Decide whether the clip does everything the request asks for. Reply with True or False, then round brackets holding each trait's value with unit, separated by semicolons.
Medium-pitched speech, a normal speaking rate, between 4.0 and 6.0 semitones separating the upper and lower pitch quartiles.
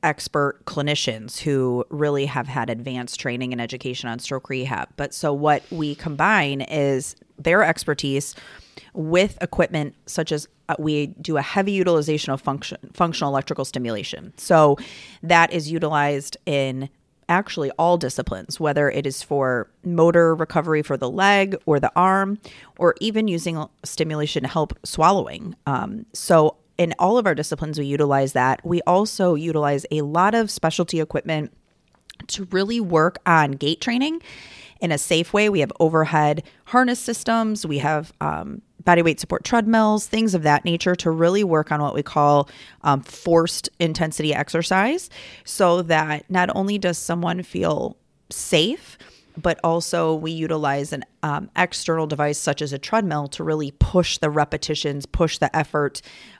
False (155 Hz; 155 wpm; 3.4 semitones)